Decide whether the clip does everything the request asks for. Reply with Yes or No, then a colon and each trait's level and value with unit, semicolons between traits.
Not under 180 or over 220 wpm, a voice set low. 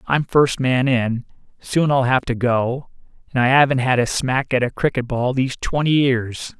Yes: average, 200 wpm; low, 130 Hz